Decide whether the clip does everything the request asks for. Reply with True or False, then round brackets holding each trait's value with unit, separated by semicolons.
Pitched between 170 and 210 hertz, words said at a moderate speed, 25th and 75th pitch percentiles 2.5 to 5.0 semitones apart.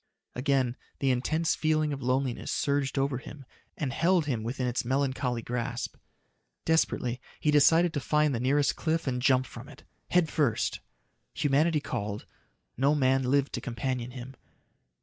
False (135 Hz; 150 wpm; 3.0 semitones)